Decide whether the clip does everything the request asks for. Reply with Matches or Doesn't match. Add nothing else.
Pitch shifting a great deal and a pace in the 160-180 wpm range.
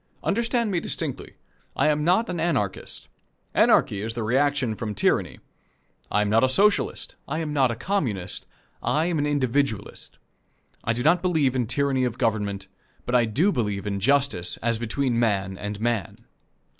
Matches